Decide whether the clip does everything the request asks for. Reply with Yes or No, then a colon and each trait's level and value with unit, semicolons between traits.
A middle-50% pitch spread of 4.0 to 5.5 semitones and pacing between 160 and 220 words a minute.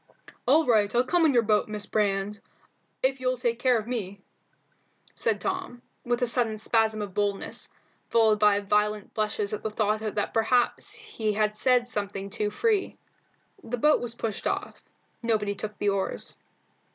No: average, 2.8 semitones; average, 165 wpm